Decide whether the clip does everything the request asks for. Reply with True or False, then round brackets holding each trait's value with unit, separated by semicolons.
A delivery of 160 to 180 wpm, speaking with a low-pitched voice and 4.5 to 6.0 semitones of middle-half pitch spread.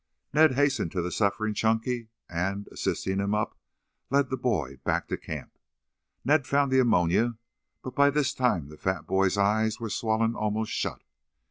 True (170 wpm; 110 Hz; 4.9 semitones)